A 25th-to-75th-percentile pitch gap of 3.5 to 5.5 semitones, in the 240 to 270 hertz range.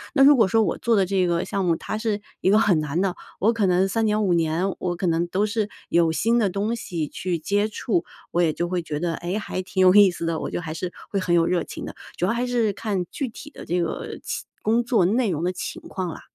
No: average, 3.8 semitones; medium, 185 Hz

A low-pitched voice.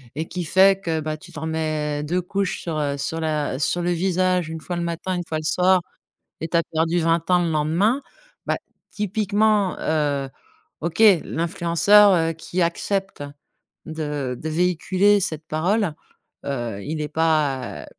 No: medium, 165 Hz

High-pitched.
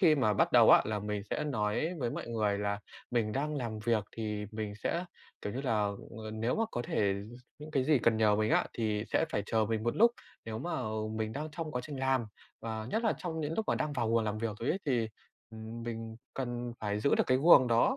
No: low, 115 Hz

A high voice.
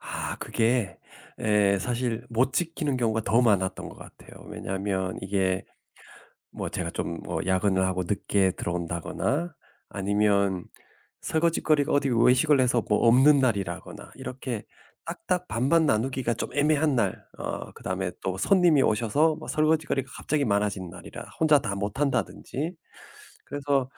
No: low, 115 Hz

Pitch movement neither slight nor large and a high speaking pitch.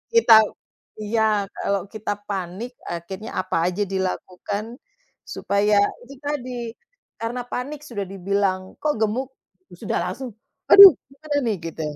Yes: average, 4.4 semitones; high, 210 Hz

